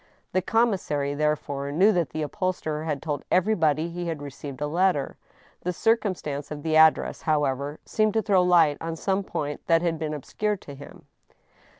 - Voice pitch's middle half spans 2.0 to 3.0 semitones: No, average, 4.0 semitones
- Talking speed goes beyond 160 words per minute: Yes, average, 180 wpm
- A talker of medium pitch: Yes, medium, 160 Hz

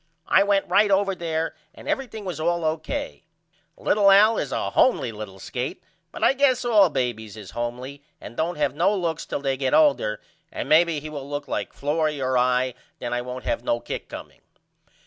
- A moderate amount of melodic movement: No, wide, 7.6 semitones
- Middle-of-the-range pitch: Yes, medium, 155 Hz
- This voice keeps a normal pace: Yes, average, 195 wpm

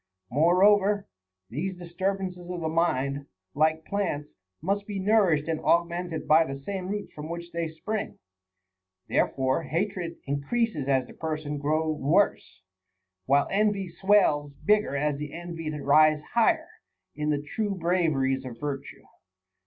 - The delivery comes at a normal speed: Yes, average, 145 wpm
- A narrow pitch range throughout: No, average, 4.5 semitones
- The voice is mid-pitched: Yes, medium, 165 Hz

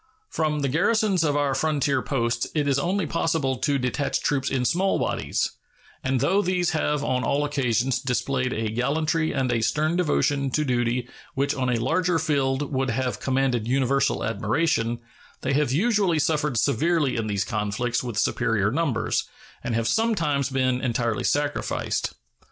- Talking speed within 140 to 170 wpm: Yes, average, 160 wpm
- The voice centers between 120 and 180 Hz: Yes, low, 135 Hz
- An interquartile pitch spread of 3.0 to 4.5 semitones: Yes, average, 3.9 semitones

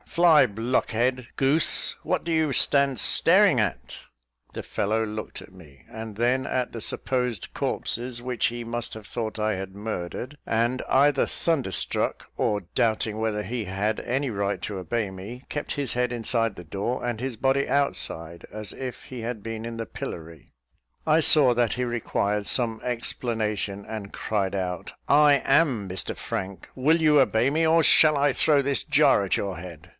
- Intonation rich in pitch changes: No, average, 4.4 semitones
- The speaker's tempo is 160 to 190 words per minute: Yes, average, 170 wpm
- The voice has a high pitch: No, low, 115 Hz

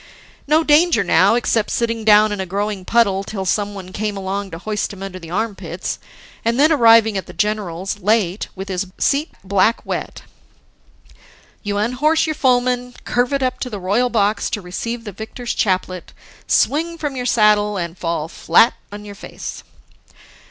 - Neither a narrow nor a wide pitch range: Yes, average, 4.0 semitones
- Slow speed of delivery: No, average, 165 wpm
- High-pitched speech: Yes, high, 210 Hz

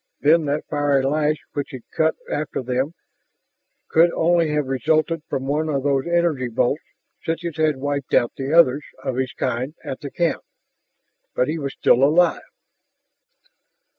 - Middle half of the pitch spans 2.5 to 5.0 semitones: Yes, average, 3.0 semitones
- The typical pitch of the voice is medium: Yes, medium, 145 Hz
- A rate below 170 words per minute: Yes, average, 160 wpm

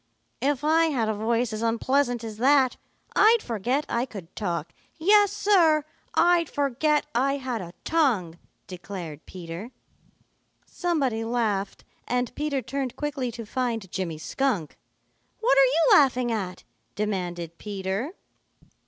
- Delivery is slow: Yes, slow, 130 wpm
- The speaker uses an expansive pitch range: Yes, wide, 6.1 semitones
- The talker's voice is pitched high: Yes, high, 240 Hz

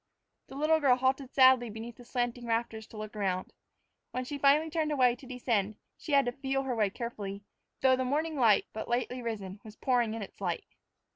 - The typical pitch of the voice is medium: No, high, 245 Hz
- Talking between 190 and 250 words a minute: Yes, fast, 205 wpm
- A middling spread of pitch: Yes, average, 3.5 semitones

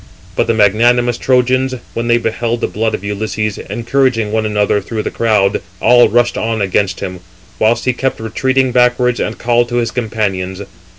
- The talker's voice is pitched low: Yes, low, 115 Hz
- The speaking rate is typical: Yes, average, 175 wpm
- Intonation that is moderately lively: No, narrow, 2.3 semitones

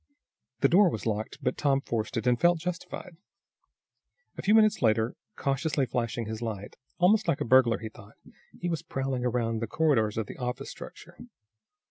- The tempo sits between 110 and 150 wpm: No, average, 175 wpm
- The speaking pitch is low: Yes, low, 125 Hz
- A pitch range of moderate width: No, wide, 6.1 semitones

